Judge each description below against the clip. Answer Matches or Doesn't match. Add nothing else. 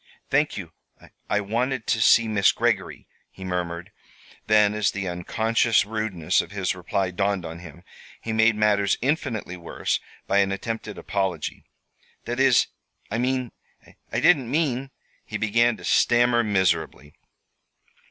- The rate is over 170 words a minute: Doesn't match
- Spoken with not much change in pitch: Doesn't match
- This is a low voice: Matches